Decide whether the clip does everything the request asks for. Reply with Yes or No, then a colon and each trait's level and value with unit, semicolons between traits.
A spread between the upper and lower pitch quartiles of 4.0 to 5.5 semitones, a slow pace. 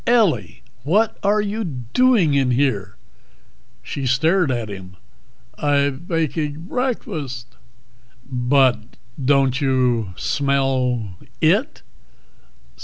Yes: average, 4.9 semitones; slow, 90 wpm